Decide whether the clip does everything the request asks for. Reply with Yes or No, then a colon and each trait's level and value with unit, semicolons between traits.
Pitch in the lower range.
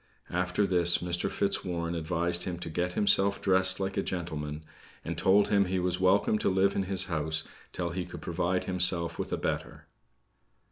Yes: very low, 90 Hz